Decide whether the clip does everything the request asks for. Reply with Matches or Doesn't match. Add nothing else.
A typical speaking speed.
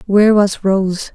Matches